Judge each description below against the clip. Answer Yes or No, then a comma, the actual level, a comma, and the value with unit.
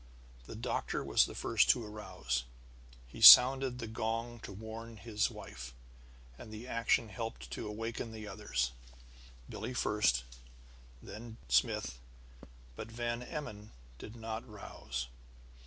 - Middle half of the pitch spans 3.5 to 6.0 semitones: No, average, 3.1 semitones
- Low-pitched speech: Yes, low, 110 Hz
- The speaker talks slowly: Yes, slow, 125 wpm